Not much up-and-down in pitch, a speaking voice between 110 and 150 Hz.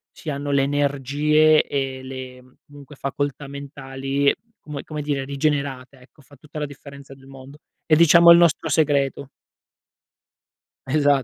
Yes: narrow, 1.6 semitones; medium, 140 Hz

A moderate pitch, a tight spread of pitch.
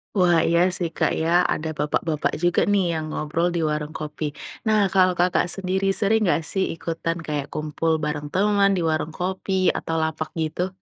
No: medium, 170 Hz; average, 3.0 semitones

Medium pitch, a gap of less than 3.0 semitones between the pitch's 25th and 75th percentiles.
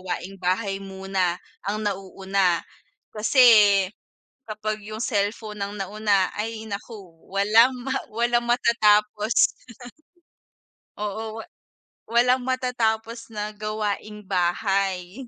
No: high, 210 Hz; narrow, 2.4 semitones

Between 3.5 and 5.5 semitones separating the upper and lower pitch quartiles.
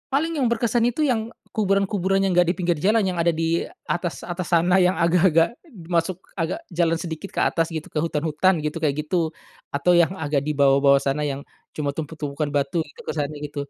Yes: average, 3.9 semitones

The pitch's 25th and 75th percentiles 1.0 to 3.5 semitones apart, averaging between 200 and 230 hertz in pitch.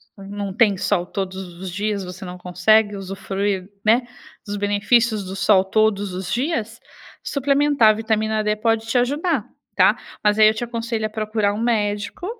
Yes: narrow, 2.4 semitones; high, 210 Hz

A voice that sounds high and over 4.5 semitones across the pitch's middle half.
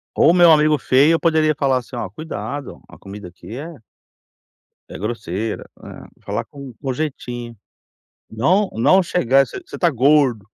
No: low, 135 Hz; average, 5.0 semitones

